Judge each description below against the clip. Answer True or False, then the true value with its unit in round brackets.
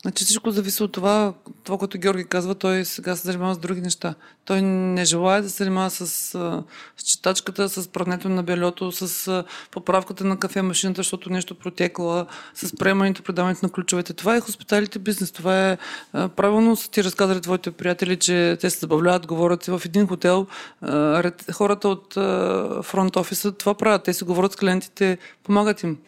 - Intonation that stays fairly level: True (1.5 semitones)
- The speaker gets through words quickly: True (175 wpm)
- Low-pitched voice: False (185 Hz)